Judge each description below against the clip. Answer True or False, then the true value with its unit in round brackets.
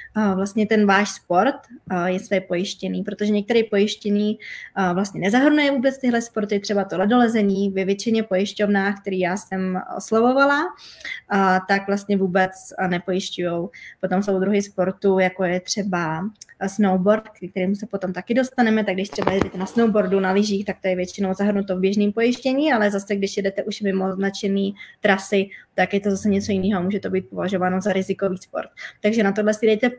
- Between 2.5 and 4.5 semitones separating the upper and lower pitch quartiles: False (2.0 semitones)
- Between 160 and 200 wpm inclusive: True (170 wpm)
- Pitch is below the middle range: False (195 Hz)